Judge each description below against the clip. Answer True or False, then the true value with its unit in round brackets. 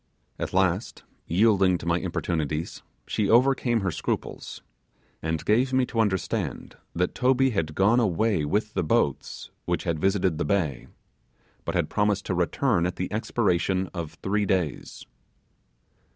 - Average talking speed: True (145 wpm)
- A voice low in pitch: True (95 Hz)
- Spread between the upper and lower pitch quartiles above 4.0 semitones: True (4.4 semitones)